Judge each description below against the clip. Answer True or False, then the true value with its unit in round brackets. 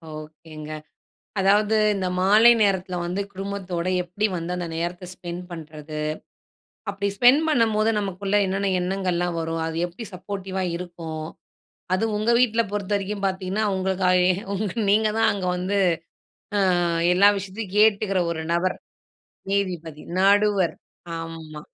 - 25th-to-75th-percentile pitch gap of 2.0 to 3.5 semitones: True (2.8 semitones)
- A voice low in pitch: False (190 Hz)